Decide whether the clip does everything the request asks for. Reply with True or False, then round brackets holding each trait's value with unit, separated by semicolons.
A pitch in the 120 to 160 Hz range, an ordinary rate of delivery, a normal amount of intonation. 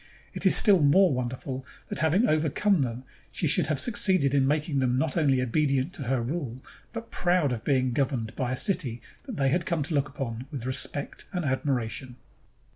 True (140 Hz; 195 wpm; 3.9 semitones)